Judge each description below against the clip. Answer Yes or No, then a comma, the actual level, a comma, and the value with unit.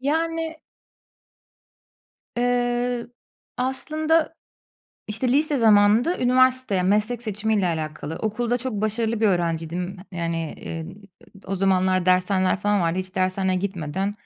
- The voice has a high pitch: Yes, high, 205 Hz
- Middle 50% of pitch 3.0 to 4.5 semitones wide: No, average, 5.0 semitones